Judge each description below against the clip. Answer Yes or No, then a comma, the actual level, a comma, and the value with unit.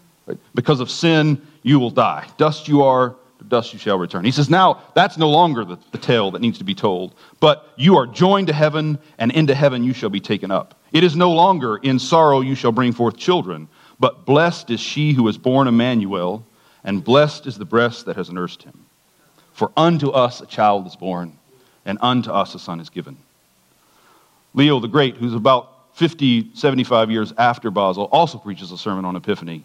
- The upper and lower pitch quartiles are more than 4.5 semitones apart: Yes, average, 5.3 semitones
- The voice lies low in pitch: Yes, low, 130 Hz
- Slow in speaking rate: No, average, 200 wpm